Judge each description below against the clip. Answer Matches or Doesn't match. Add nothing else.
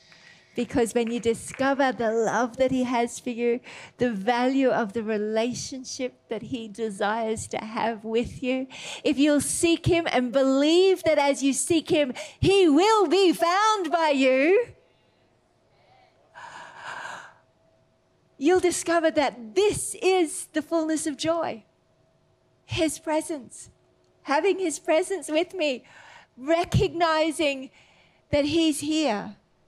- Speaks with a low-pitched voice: Doesn't match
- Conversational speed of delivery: Doesn't match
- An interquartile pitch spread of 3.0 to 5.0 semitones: Doesn't match